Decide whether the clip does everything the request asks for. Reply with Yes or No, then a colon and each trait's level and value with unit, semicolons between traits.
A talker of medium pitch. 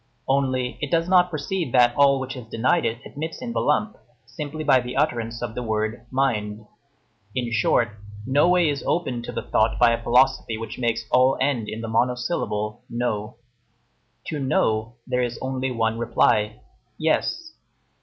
No: low, 125 Hz